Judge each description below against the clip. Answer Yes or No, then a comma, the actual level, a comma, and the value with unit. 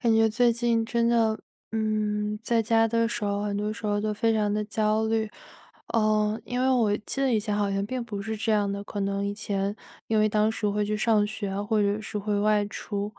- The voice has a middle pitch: No, high, 215 Hz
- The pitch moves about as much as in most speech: No, narrow, 1.5 semitones